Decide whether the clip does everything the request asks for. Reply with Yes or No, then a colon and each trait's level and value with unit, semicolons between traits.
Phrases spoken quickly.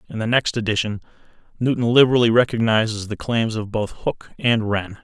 No: average, 165 wpm